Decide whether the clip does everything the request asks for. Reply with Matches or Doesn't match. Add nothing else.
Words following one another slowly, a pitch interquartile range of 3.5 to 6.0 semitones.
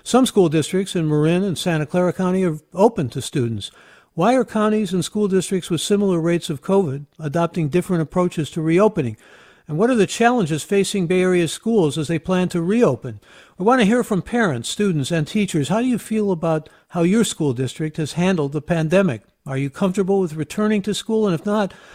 Doesn't match